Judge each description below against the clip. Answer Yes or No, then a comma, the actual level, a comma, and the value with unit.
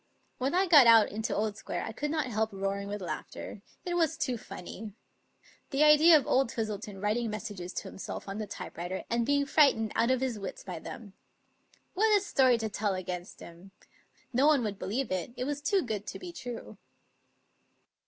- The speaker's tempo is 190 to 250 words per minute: Yes, average, 195 wpm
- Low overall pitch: No, high, 225 Hz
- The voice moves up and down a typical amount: No, wide, 5.8 semitones